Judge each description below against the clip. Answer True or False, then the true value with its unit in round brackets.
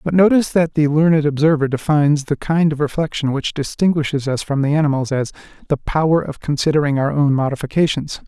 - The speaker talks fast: False (180 wpm)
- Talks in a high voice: False (150 Hz)